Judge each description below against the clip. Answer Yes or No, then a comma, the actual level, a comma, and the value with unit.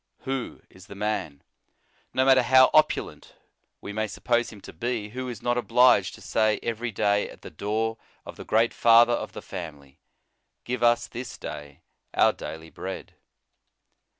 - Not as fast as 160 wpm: No, average, 165 wpm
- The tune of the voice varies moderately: Yes, average, 3.3 semitones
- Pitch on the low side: Yes, low, 115 Hz